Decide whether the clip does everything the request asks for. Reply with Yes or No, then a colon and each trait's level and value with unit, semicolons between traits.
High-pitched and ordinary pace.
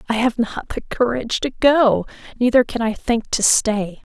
Yes: high, 235 Hz; average, 190 wpm